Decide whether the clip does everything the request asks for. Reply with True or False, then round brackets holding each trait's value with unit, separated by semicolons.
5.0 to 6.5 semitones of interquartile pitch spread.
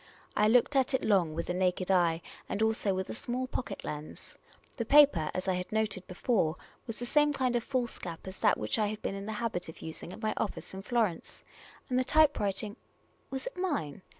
True (5.3 semitones)